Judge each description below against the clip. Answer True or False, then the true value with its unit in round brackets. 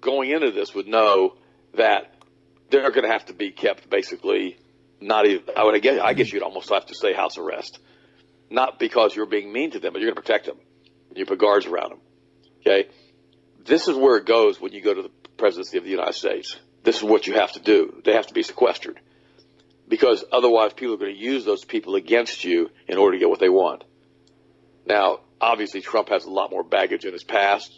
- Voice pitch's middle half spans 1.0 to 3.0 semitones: True (2.4 semitones)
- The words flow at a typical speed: False (225 wpm)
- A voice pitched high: True (400 Hz)